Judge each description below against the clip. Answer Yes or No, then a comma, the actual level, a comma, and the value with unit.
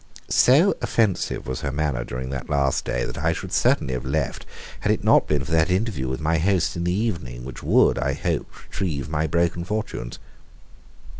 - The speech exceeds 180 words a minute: Yes, average, 195 wpm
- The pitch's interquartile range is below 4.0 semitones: No, average, 5.0 semitones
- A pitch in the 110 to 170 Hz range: No, very low, 75 Hz